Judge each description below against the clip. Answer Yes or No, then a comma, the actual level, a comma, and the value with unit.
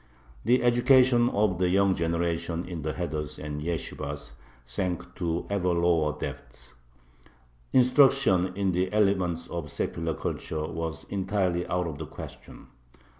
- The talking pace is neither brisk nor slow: No, slow, 130 wpm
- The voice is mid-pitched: No, very low, 90 Hz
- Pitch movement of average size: Yes, average, 3.4 semitones